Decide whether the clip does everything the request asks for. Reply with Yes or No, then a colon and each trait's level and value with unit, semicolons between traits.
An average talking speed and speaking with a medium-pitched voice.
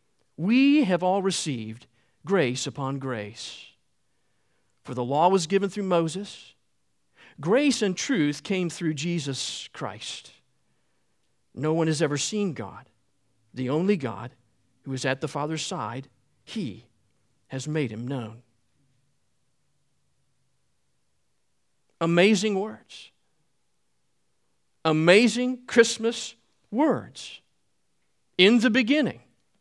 No: slow, 100 wpm; medium, 145 Hz